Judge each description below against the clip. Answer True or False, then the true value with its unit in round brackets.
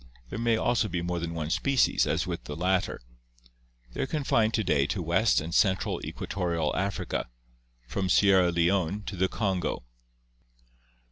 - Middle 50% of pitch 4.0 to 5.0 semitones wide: False (3.6 semitones)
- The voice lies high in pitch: False (95 Hz)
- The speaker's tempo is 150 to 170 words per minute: True (160 wpm)